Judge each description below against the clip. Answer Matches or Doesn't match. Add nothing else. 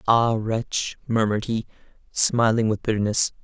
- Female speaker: Doesn't match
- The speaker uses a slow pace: Matches